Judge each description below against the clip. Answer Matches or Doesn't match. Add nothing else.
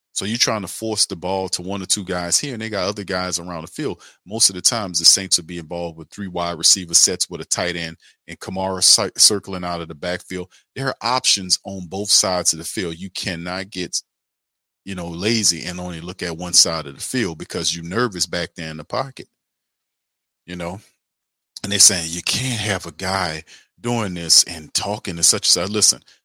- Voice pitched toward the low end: Matches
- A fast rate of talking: Matches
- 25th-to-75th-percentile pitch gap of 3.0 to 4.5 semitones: Doesn't match